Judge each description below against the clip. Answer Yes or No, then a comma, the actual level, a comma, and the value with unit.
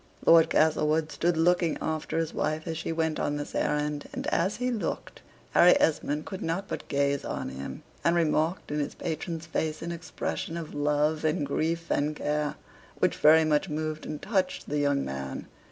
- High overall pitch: No, medium, 155 Hz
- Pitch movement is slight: Yes, narrow, 1.9 semitones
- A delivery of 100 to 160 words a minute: No, average, 185 wpm